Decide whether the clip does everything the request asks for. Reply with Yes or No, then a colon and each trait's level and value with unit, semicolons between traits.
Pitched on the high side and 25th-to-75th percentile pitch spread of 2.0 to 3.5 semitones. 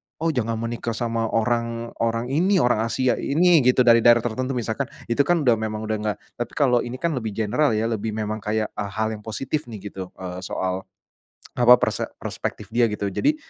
No: low, 115 Hz; narrow, 2.6 semitones